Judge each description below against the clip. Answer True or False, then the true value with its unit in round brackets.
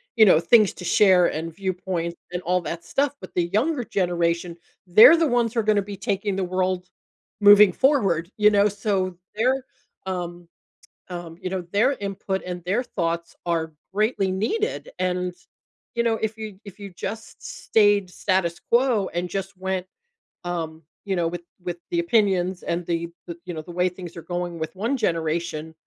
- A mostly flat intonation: False (3.3 semitones)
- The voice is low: False (185 Hz)